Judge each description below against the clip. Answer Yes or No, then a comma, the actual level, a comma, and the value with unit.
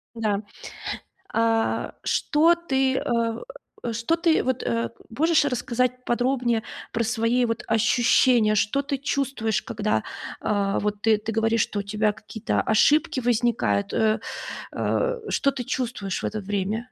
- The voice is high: Yes, high, 230 Hz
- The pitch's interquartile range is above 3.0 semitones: Yes, average, 3.5 semitones